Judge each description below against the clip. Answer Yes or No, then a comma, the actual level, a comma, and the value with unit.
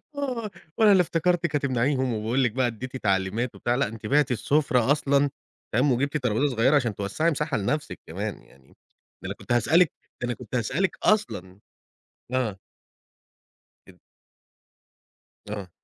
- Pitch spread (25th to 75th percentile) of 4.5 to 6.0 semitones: Yes, average, 4.9 semitones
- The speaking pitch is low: Yes, low, 130 Hz